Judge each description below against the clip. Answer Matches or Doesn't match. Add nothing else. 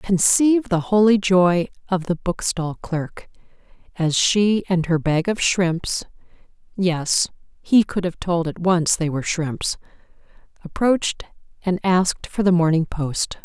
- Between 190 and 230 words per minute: Doesn't match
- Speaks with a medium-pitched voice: Matches